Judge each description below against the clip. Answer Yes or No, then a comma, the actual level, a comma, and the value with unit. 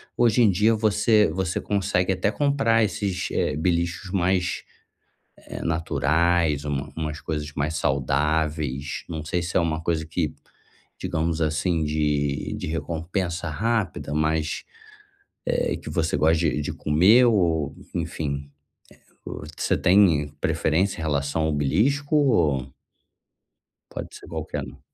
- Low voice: Yes, very low, 80 Hz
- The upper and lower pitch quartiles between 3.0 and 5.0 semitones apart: Yes, average, 4.0 semitones